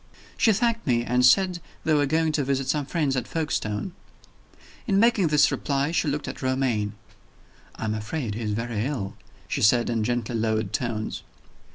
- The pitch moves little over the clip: No, wide, 5.6 semitones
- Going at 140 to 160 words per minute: No, average, 180 wpm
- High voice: No, low, 130 Hz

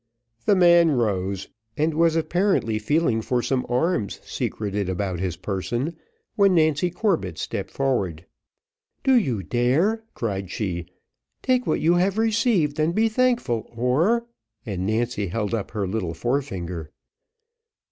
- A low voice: Yes, low, 125 Hz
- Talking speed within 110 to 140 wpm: Yes, slow, 135 wpm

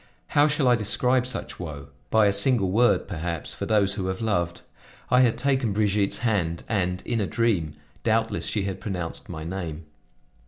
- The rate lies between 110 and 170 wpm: No, average, 180 wpm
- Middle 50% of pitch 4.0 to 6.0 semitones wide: Yes, average, 4.5 semitones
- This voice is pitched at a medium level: No, low, 100 Hz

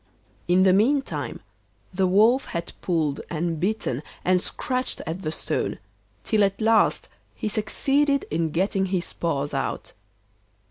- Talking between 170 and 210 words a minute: No, slow, 135 wpm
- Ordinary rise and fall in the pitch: Yes, average, 4.6 semitones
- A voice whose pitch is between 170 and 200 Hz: Yes, high, 190 Hz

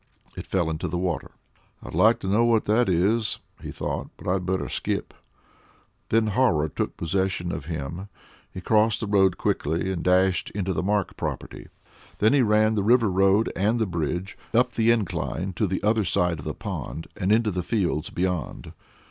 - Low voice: Yes, very low, 95 Hz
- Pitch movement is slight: No, average, 3.5 semitones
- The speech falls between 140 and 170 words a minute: No, average, 185 wpm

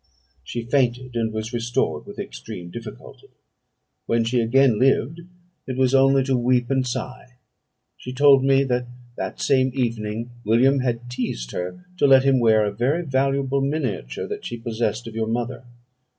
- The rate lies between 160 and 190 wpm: Yes, average, 165 wpm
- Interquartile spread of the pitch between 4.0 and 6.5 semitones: No, average, 2.7 semitones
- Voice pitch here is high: No, low, 125 Hz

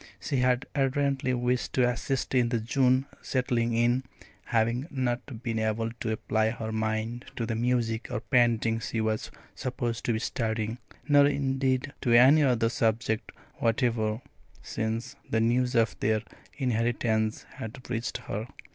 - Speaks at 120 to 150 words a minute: Yes, average, 145 wpm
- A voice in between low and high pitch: No, low, 120 Hz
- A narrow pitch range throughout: Yes, narrow, 2.2 semitones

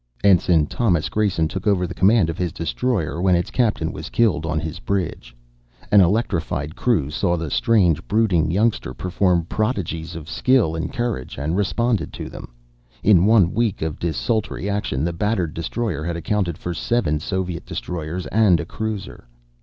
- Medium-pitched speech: No, very low, 90 Hz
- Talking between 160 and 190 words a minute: Yes, average, 165 wpm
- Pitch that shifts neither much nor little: Yes, average, 4.6 semitones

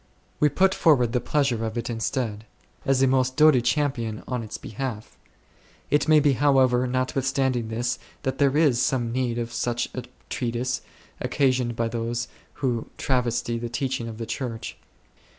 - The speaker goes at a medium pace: Yes, average, 170 wpm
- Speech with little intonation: Yes, narrow, 2.3 semitones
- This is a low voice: Yes, low, 125 Hz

